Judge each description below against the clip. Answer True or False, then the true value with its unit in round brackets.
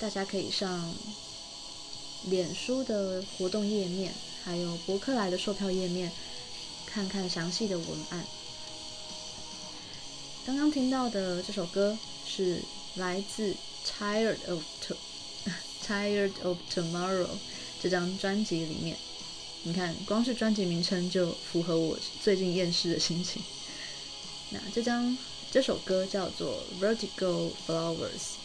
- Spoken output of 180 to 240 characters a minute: True (235 characters per minute)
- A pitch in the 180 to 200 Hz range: True (190 Hz)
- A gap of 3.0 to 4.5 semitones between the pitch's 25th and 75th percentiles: False (2.6 semitones)